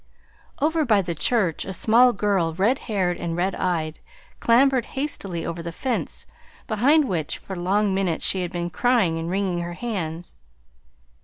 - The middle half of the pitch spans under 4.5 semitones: No, wide, 5.4 semitones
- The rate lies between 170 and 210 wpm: No, average, 160 wpm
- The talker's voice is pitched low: No, high, 190 Hz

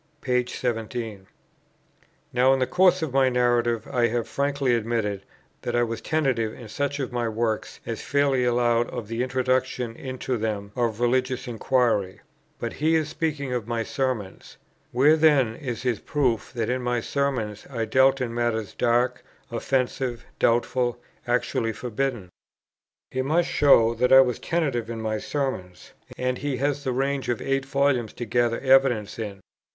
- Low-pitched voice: Yes, low, 125 Hz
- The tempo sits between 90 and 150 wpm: No, average, 160 wpm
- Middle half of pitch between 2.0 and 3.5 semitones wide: Yes, narrow, 2.6 semitones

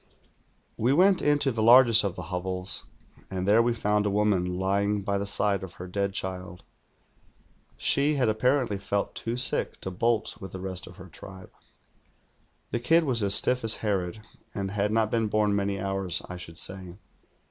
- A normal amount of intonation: Yes, average, 3.4 semitones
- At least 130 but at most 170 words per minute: No, average, 185 wpm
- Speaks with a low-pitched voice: Yes, low, 100 Hz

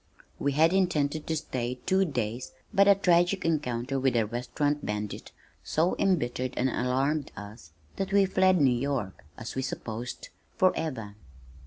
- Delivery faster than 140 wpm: Yes, average, 150 wpm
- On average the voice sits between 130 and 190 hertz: Yes, medium, 140 Hz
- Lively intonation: Yes, wide, 6.0 semitones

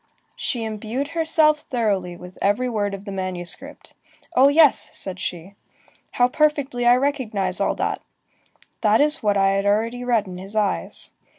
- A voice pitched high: Yes, high, 220 Hz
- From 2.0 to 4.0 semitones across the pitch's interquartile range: No, average, 5.2 semitones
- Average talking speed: Yes, average, 160 wpm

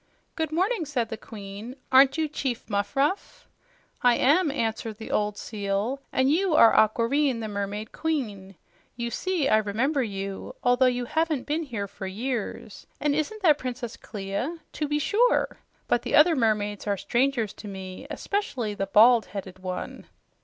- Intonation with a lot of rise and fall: Yes, wide, 6.1 semitones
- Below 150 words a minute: No, average, 160 wpm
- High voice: Yes, high, 240 Hz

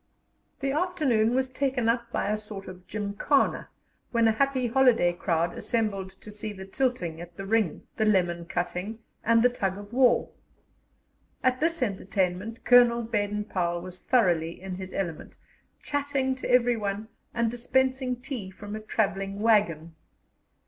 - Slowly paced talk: No, average, 150 wpm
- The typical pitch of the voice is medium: No, high, 215 Hz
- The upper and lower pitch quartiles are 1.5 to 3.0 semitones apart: No, average, 4.6 semitones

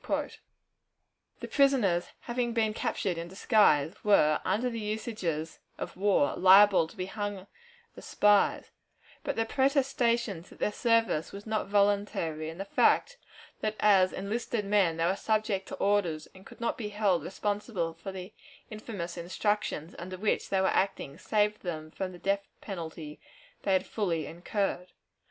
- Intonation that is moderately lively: Yes, average, 3.5 semitones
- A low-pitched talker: No, high, 200 Hz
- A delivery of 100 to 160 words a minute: Yes, average, 155 wpm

